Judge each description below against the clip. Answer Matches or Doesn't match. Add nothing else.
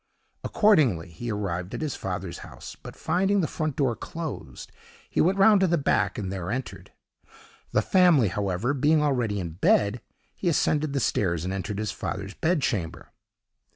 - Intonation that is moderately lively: Doesn't match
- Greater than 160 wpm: Matches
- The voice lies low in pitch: Matches